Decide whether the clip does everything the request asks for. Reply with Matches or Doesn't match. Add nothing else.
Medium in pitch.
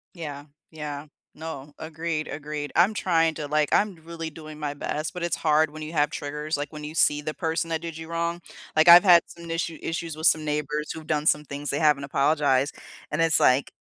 Matches